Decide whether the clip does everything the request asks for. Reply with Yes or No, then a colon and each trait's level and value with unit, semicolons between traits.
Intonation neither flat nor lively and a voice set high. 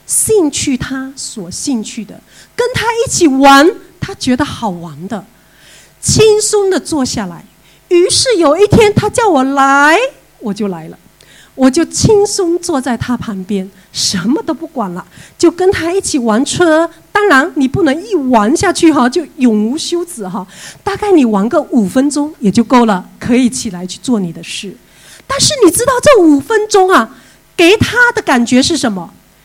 No: wide, 7.7 semitones; very high, 280 Hz